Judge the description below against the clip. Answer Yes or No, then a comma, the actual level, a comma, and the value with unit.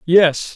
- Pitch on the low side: No, medium, 170 Hz